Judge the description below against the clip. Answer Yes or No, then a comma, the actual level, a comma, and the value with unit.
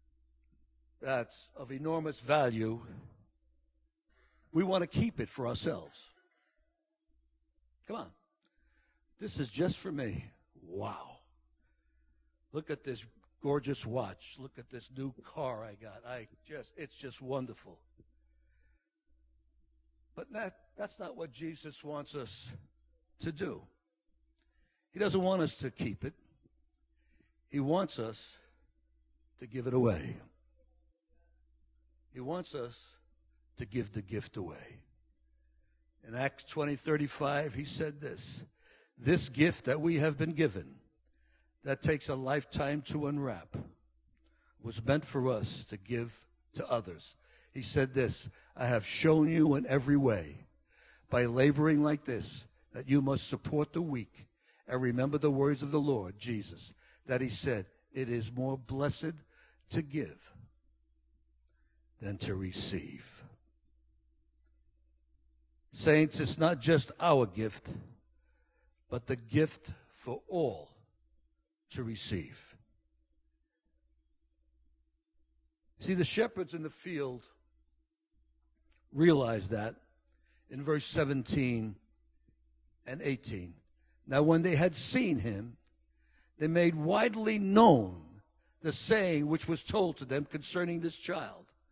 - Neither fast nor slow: No, slow, 120 wpm